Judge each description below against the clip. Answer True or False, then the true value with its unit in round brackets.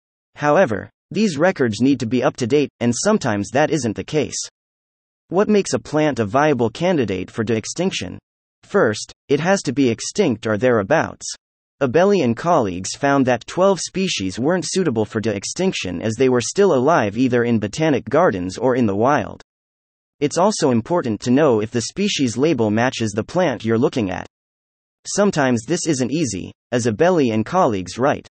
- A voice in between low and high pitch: False (130 Hz)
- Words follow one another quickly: False (175 wpm)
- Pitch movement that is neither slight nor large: False (6.5 semitones)